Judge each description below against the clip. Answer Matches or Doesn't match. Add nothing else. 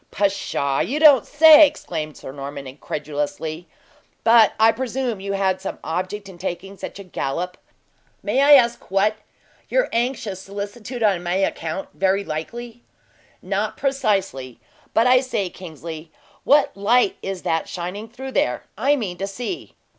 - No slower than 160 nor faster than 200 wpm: Doesn't match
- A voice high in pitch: Matches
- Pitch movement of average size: Doesn't match